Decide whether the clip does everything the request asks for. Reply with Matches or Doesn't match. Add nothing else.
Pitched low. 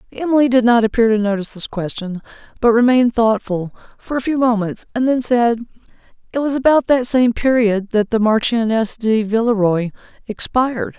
Doesn't match